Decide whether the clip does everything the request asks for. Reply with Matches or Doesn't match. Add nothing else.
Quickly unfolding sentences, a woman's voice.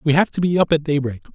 Doesn't match